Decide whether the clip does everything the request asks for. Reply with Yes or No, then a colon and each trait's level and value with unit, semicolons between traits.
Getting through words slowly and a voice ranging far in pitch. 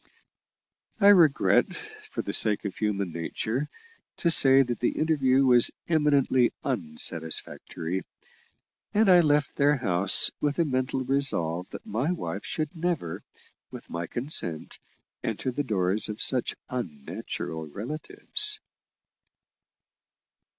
Yes: slow, 115 wpm; wide, 7.5 semitones